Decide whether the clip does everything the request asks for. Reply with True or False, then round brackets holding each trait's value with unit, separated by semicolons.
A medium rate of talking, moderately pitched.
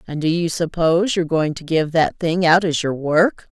False (235 wpm; 165 Hz)